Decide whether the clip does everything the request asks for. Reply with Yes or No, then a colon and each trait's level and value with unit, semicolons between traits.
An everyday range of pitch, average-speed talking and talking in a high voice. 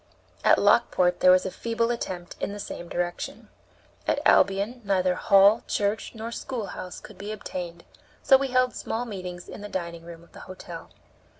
Yes: average, 3.8 semitones; average, 175 wpm; high, 195 Hz